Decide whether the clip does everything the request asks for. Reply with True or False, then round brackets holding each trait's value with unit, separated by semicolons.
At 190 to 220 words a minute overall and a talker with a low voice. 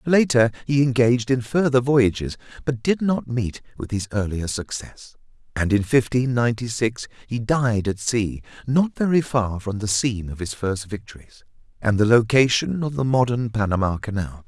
False (170 wpm; 115 Hz)